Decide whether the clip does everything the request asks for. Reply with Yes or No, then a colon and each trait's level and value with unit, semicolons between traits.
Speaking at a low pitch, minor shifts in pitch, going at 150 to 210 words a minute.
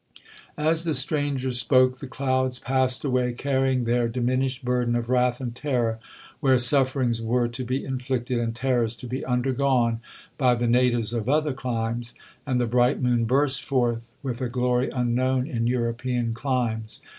Yes: low, 125 Hz; narrow, 1.7 semitones; average, 155 wpm